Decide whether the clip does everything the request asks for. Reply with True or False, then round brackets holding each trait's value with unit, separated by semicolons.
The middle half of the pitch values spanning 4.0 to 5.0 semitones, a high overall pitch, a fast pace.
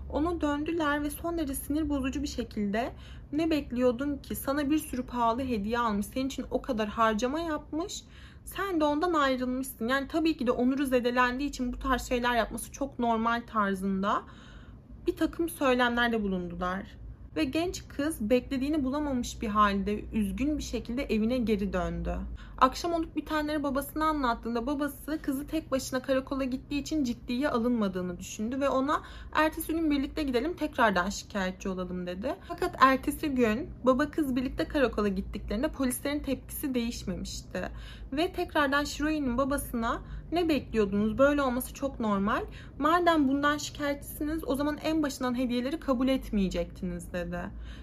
True (4.3 semitones; 265 Hz; 145 wpm)